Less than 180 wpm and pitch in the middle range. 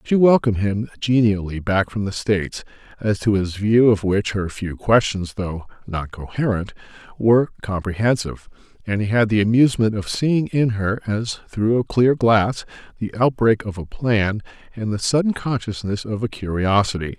No: average, 170 wpm; low, 105 Hz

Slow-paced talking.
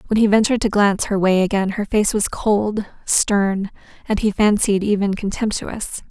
No: average, 175 wpm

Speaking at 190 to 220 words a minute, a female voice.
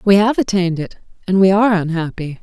Yes: average, 200 wpm; female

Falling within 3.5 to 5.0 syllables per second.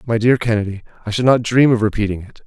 No: 6.7 syllables/s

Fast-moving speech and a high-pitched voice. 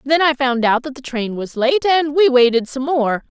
Yes: fast, 250 wpm; very high, 270 Hz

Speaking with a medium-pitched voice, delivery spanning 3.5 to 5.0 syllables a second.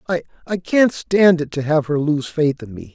Yes: medium, 160 Hz; 4.8 syllables/s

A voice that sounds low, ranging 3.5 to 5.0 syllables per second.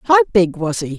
No: high, 210 Hz; 4.9 syllables/s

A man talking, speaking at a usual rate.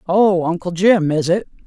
No: female; average, 180 wpm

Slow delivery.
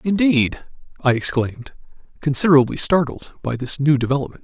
Yes: slow, 120 wpm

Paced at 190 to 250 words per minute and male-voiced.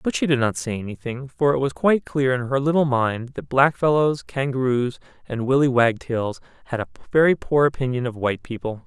Yes: average, 195 wpm; male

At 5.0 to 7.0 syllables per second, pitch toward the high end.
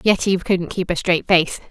No: 5.2 syllables/s; medium, 180 Hz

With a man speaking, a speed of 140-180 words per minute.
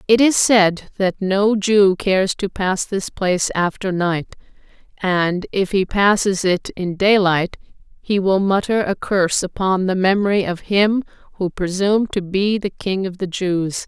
No: female; average, 170 wpm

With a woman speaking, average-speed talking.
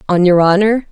Yes: female; average, 195 wpm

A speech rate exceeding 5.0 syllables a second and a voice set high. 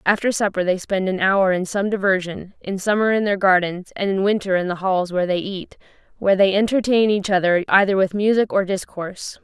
Yes: 5.6 syllables/s; high, 195 Hz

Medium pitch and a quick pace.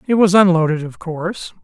No: medium, 175 Hz; average, 185 wpm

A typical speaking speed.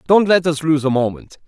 No: fast, 245 wpm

